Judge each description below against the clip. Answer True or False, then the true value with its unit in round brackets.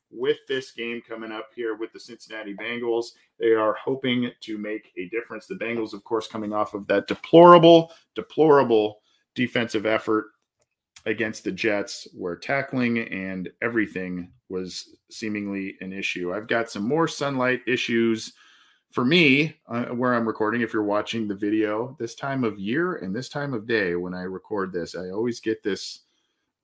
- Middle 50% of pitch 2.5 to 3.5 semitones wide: True (2.8 semitones)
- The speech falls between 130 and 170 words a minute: True (165 wpm)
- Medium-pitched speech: False (115 Hz)